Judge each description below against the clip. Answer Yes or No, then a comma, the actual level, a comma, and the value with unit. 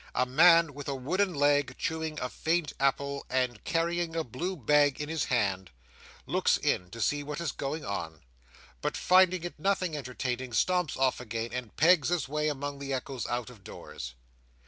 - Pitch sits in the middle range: Yes, medium, 145 Hz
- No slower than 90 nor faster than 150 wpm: No, average, 180 wpm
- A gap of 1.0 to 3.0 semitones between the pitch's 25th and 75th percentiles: No, average, 4.4 semitones